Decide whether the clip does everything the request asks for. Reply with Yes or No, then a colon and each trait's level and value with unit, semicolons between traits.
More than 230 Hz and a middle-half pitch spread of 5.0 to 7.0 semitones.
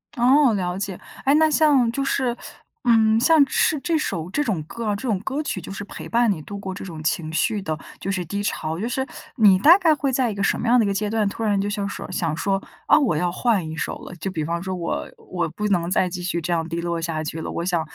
No: high, 200 Hz; wide, 5.6 semitones